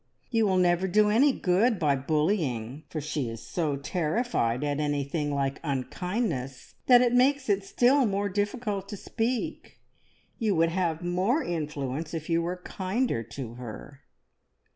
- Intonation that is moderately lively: No, wide, 6.6 semitones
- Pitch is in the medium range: Yes, medium, 175 Hz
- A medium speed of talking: Yes, average, 150 wpm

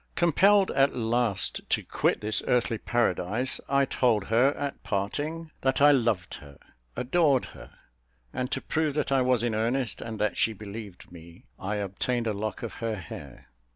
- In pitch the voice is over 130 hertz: No, low, 115 Hz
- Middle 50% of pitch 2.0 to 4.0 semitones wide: No, average, 4.5 semitones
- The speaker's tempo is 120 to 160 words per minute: No, average, 170 wpm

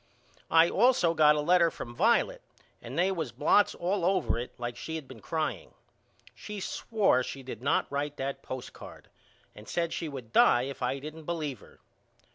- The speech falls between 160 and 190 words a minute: Yes, average, 185 wpm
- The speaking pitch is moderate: Yes, medium, 155 Hz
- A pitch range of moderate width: Yes, average, 5.0 semitones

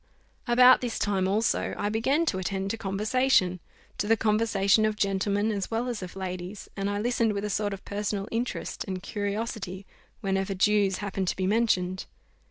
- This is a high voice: Yes, high, 205 Hz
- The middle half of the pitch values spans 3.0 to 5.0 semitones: No, narrow, 2.5 semitones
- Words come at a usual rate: Yes, average, 180 wpm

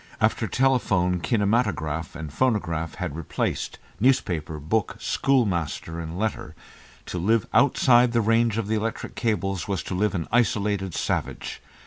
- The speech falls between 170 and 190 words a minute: No, slow, 135 wpm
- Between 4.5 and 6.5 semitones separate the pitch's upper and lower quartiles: Yes, wide, 5.4 semitones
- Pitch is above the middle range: No, low, 100 Hz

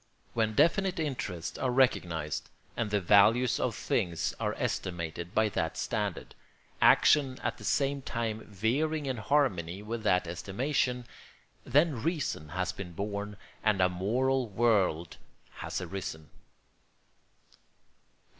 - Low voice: Yes, low, 110 Hz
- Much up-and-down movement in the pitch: Yes, wide, 6.3 semitones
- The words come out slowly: Yes, slow, 120 wpm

